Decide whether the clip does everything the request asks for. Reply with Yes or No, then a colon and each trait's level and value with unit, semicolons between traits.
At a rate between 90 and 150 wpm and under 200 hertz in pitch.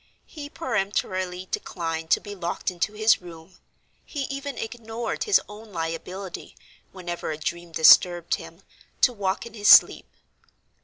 Yes: average, 140 wpm; high, 190 Hz